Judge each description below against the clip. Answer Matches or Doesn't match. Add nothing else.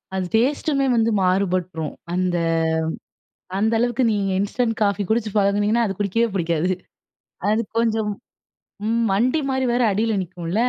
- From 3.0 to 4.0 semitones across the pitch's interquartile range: Matches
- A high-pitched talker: Matches